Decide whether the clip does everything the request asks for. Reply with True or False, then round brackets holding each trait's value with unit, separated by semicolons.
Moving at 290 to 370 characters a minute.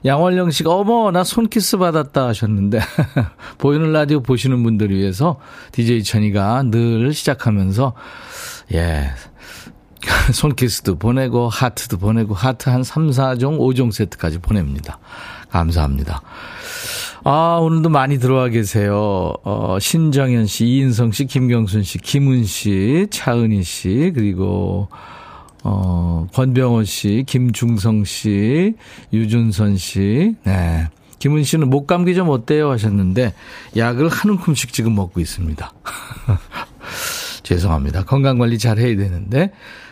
False (255 characters per minute)